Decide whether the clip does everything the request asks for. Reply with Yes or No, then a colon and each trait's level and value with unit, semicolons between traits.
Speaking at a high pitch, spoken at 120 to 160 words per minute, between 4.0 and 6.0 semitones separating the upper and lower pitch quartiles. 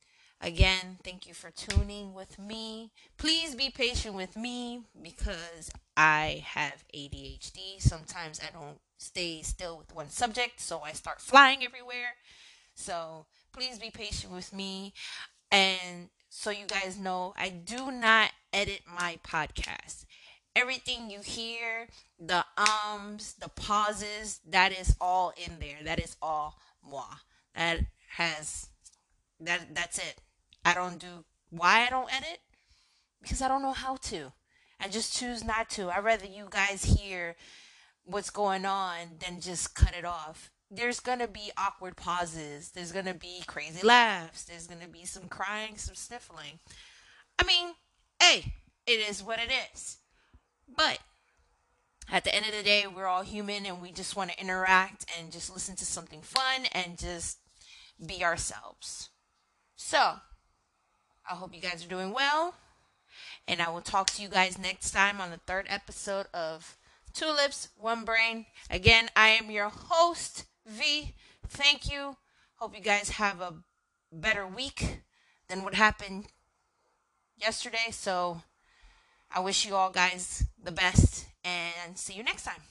Yes: high, 195 Hz; average, 150 wpm; average, 4.4 semitones